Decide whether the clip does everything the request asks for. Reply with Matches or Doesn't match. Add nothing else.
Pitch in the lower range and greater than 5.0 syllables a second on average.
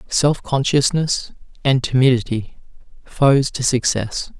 Doesn't match